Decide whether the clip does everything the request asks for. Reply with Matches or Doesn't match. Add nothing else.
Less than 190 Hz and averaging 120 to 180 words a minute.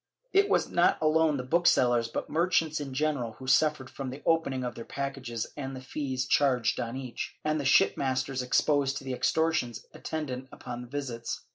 Doesn't match